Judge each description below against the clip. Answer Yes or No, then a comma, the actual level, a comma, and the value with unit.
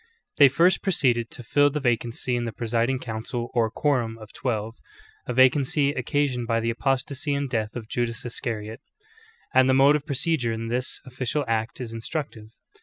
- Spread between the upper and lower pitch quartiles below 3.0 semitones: No, average, 3.3 semitones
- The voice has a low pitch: Yes, low, 125 Hz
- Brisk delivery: No, average, 175 wpm